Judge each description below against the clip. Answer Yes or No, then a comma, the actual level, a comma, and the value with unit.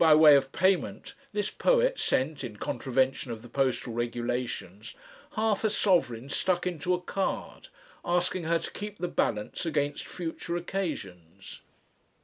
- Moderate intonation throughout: No, wide, 6.9 semitones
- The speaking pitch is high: No, medium, 155 Hz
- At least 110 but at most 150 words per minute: Yes, average, 140 wpm